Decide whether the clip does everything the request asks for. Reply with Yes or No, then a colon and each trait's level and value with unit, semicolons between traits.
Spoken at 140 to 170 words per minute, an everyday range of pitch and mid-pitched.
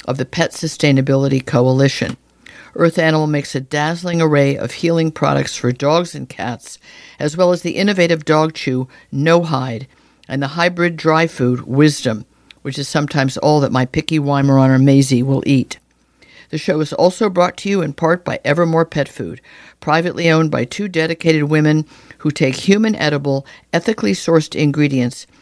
Yes: average, 165 wpm; average, 3.4 semitones; medium, 150 Hz